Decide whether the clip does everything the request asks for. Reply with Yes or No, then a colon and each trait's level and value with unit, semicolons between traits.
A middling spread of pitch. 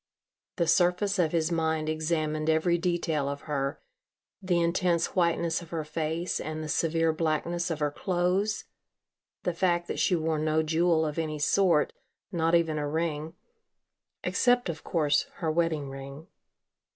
No: narrow, 1.9 semitones